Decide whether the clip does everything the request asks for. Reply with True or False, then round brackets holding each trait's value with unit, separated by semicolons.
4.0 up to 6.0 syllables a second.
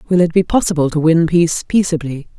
False (6.2 syllables/s)